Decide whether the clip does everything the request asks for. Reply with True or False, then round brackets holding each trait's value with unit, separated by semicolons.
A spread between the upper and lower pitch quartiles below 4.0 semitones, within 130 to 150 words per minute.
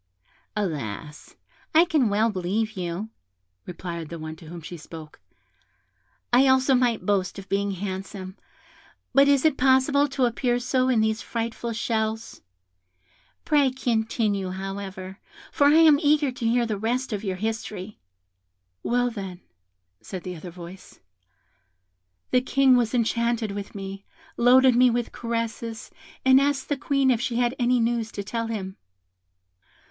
False (4.6 semitones; 145 wpm)